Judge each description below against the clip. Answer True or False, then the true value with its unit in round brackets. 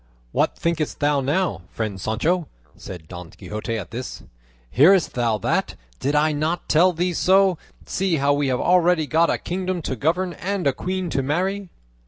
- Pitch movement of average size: False (5.7 semitones)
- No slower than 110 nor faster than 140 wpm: False (175 wpm)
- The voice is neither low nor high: True (155 Hz)